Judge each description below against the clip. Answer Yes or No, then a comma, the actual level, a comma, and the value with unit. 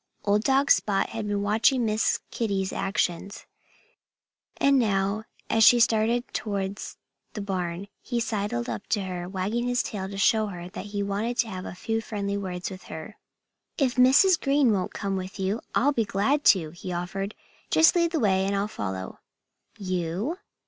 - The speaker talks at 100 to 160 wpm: No, average, 175 wpm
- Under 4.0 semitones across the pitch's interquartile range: Yes, average, 3.3 semitones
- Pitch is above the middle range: Yes, high, 205 Hz